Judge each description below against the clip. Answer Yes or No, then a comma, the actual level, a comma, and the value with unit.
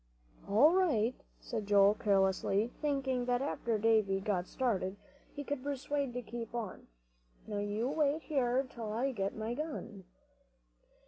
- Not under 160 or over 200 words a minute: No, average, 145 wpm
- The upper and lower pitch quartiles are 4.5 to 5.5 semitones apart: Yes, average, 4.8 semitones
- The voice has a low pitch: No, high, 235 Hz